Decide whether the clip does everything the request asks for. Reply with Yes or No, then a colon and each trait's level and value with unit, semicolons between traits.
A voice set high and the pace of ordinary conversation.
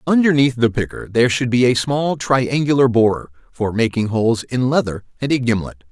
No: low, 120 Hz; average, 185 wpm